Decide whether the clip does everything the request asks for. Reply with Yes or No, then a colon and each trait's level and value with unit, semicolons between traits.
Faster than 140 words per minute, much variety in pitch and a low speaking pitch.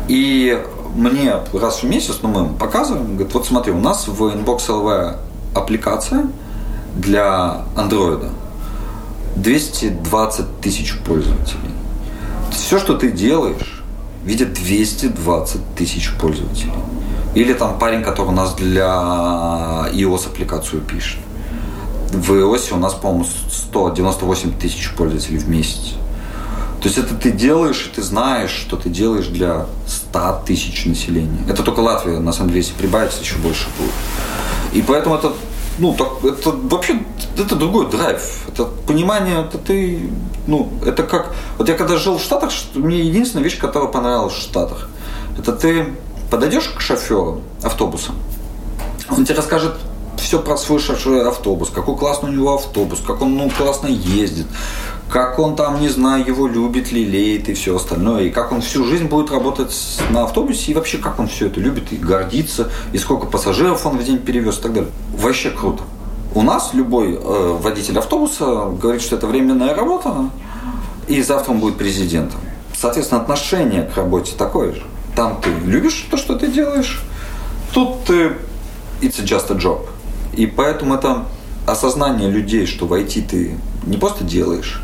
Yes: average, 155 wpm; wide, 7.5 semitones; low, 110 Hz